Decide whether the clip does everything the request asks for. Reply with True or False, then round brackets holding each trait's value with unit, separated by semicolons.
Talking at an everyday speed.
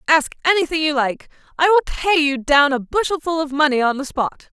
False (210 wpm)